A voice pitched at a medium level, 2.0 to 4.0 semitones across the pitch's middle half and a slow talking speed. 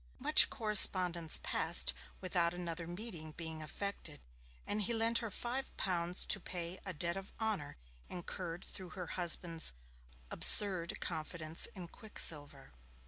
Yes: medium, 175 Hz; average, 3.0 semitones; slow, 130 wpm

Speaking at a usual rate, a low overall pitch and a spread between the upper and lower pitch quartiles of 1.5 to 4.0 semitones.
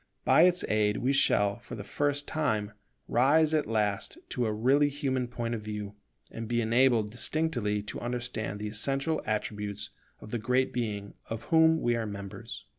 No: average, 175 wpm; low, 120 Hz; average, 4.5 semitones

